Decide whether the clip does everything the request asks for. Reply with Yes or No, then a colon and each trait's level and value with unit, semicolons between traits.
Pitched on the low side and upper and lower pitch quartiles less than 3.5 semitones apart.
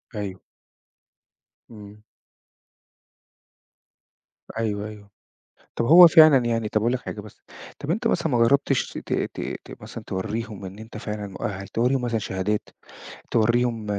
Yes: low, 110 Hz; average, 3.0 semitones